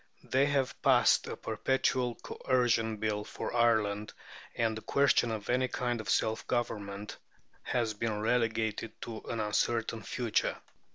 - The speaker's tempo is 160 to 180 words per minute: No, slow, 135 wpm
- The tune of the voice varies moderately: No, narrow, 2.2 semitones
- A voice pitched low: Yes, low, 115 Hz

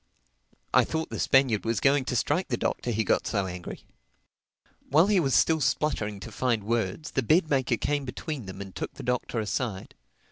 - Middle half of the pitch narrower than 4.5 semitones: No, wide, 5.4 semitones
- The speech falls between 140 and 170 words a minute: No, average, 190 wpm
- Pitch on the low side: Yes, low, 125 Hz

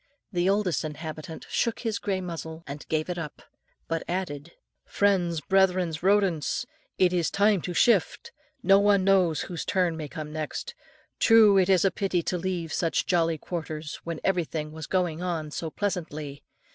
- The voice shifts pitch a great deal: No, average, 3.2 semitones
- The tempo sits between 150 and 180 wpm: Yes, average, 165 wpm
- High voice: No, medium, 175 Hz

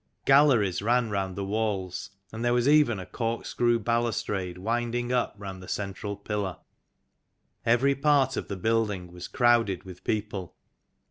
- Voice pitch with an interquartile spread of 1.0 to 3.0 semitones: No, average, 3.7 semitones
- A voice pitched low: Yes, low, 110 Hz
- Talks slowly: No, average, 145 wpm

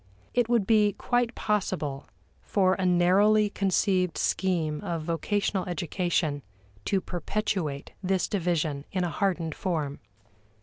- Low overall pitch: No, medium, 185 Hz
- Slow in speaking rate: Yes, slow, 120 wpm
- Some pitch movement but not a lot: Yes, average, 3.6 semitones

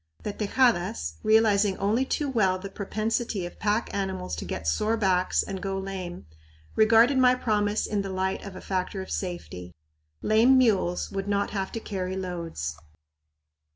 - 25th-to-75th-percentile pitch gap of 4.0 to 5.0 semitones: No, average, 2.8 semitones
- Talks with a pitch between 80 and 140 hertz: No, high, 200 Hz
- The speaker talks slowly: No, average, 160 wpm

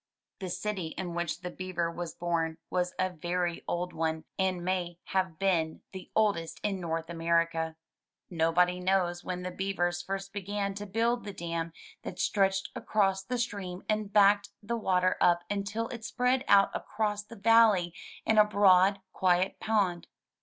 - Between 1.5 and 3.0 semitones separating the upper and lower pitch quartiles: Yes, average, 2.7 semitones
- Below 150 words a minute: No, average, 160 wpm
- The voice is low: No, medium, 185 Hz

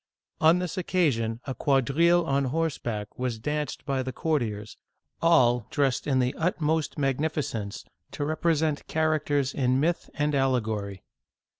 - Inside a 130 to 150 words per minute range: Yes, slow, 135 wpm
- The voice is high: No, medium, 140 Hz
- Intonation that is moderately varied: Yes, average, 4.2 semitones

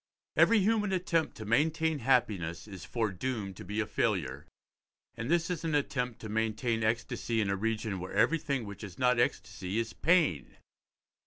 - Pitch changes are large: Yes, wide, 6.5 semitones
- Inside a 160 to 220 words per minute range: Yes, average, 165 wpm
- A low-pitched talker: Yes, low, 115 Hz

